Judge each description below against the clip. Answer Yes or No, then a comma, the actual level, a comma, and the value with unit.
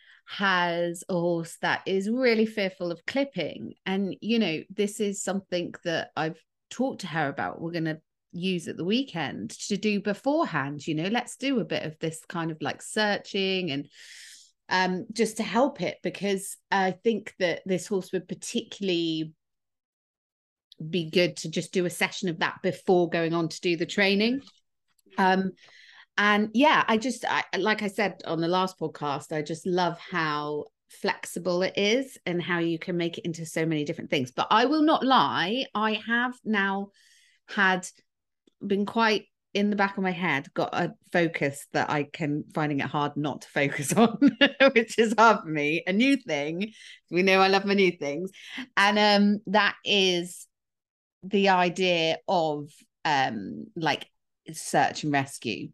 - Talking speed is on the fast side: No, average, 170 wpm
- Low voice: No, medium, 185 Hz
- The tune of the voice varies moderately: Yes, average, 4.3 semitones